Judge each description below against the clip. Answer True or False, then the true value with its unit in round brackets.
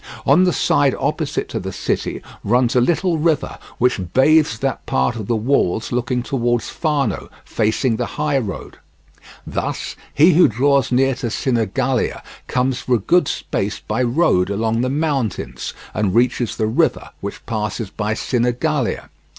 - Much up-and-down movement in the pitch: False (3.9 semitones)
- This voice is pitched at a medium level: False (125 Hz)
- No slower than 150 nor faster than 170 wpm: True (155 wpm)